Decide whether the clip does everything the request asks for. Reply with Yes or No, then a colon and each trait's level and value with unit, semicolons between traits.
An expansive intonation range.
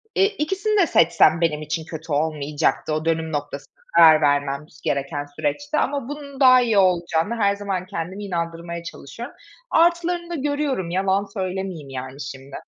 Yes: wide, 8.9 semitones